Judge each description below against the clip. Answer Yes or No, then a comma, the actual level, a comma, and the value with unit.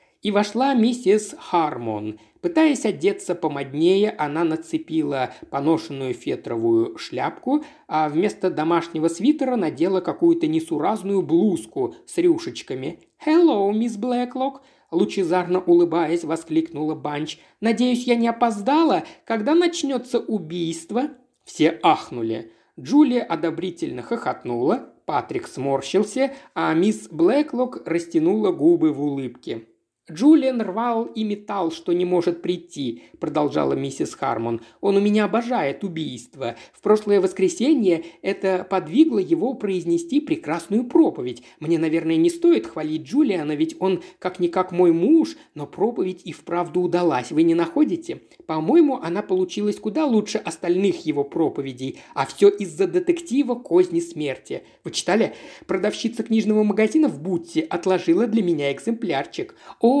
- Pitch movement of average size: No, wide, 8.6 semitones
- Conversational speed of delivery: Yes, average, 120 wpm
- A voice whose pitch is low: No, high, 200 Hz